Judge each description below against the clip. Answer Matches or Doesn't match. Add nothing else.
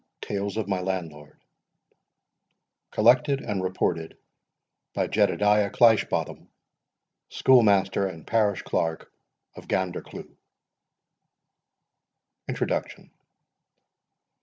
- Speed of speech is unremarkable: Doesn't match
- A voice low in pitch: Matches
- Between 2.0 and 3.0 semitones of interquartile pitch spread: Matches